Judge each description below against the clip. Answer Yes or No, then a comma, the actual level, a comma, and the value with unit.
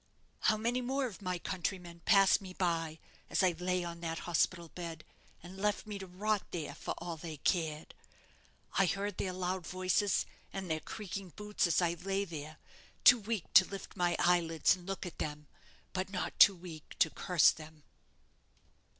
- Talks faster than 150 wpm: Yes, average, 175 wpm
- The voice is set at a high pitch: No, medium, 180 Hz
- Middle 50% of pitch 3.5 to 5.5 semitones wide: No, average, 2.7 semitones